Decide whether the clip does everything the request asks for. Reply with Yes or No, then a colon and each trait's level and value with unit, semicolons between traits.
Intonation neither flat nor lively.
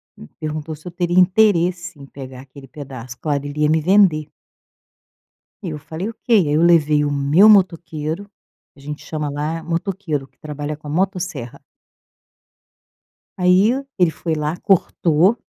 Yes: average, 3.6 semitones